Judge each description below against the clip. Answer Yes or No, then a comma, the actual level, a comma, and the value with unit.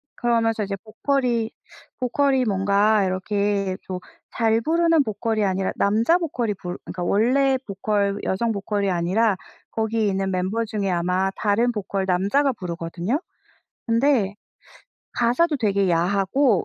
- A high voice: Yes, high, 210 Hz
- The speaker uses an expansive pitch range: No, average, 3.5 semitones